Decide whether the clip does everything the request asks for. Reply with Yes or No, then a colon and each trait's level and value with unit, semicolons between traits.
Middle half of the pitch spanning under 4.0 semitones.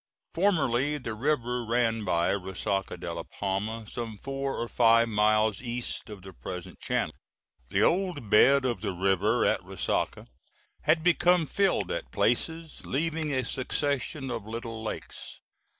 No: wide, 5.4 semitones